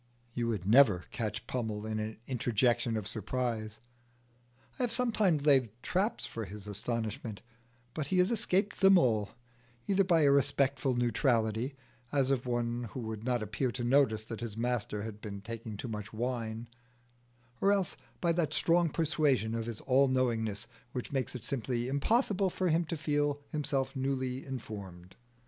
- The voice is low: Yes, low, 125 Hz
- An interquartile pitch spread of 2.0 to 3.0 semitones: No, average, 4.5 semitones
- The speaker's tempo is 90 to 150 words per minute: No, average, 160 wpm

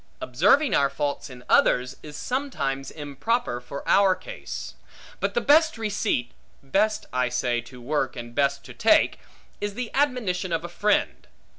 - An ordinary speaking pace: Yes, average, 155 wpm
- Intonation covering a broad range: Yes, wide, 9.0 semitones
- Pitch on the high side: No, medium, 155 Hz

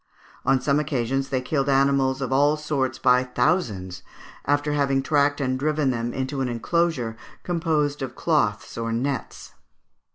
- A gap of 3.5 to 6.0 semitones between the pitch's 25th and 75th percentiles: No, narrow, 2.6 semitones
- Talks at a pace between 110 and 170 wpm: Yes, average, 150 wpm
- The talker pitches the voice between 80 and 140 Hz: Yes, low, 135 Hz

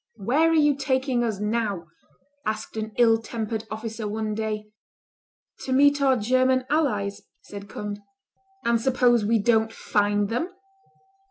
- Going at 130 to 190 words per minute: Yes, average, 140 wpm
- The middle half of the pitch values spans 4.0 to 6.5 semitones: No, average, 3.4 semitones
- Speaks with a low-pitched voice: No, high, 225 Hz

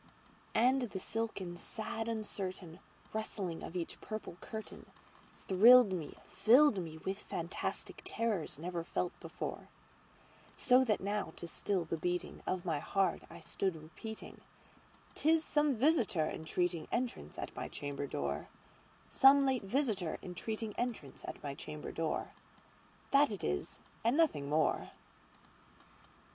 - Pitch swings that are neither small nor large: No, wide, 5.7 semitones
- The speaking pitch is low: No, high, 195 Hz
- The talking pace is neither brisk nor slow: No, slow, 120 wpm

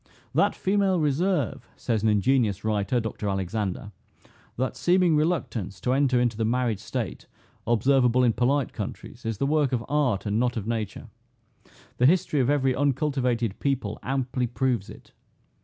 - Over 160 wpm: No, average, 155 wpm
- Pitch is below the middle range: Yes, low, 125 Hz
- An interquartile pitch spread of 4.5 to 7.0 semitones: No, average, 4.1 semitones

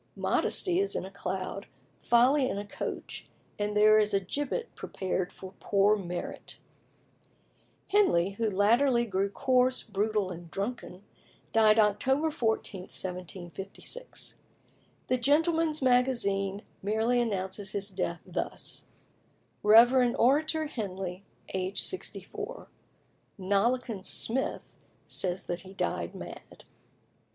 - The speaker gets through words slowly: Yes, slow, 110 wpm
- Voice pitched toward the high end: Yes, high, 210 Hz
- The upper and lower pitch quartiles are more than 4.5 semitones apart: Yes, average, 4.9 semitones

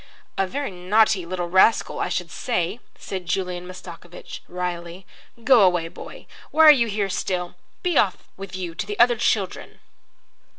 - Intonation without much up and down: No, average, 3.5 semitones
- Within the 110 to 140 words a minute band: No, average, 160 wpm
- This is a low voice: No, medium, 185 Hz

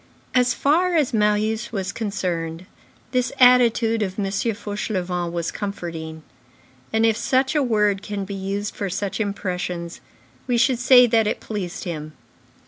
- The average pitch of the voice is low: No, high, 210 Hz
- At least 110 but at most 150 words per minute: Yes, average, 145 wpm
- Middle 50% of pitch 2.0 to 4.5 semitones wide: Yes, average, 4.1 semitones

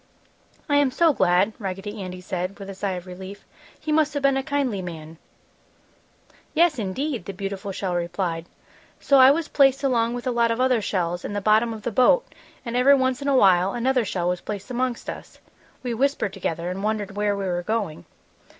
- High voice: Yes, high, 210 Hz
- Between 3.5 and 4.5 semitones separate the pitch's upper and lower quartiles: No, wide, 5.6 semitones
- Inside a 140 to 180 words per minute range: No, fast, 205 wpm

